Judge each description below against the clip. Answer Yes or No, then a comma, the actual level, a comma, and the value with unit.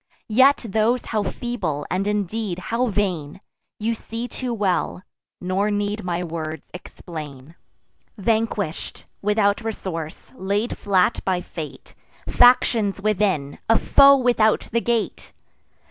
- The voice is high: Yes, high, 205 Hz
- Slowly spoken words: Yes, slow, 115 wpm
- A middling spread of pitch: Yes, average, 4.1 semitones